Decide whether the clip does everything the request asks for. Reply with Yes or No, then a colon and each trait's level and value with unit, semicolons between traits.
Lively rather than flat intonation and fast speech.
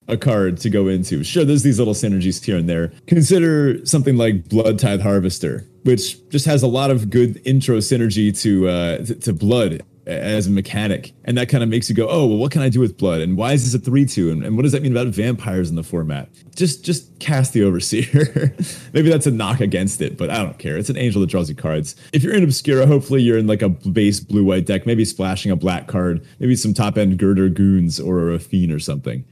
Yes: wide, 6.0 semitones; fast, 235 wpm